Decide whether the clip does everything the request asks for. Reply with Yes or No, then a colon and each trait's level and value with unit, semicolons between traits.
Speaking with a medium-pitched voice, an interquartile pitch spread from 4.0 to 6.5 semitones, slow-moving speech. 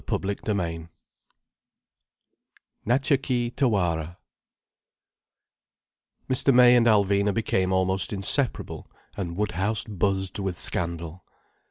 No: low, 100 Hz; average, 4.6 semitones; slow, 85 wpm